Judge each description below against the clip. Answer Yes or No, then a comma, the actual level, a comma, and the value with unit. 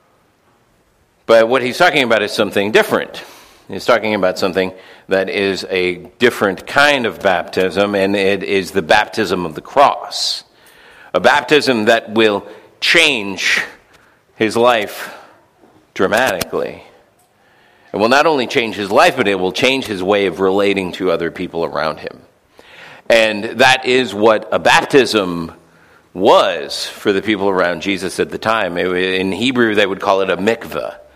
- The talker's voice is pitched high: No, low, 100 Hz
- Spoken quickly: No, average, 150 wpm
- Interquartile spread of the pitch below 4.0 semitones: Yes, average, 3.6 semitones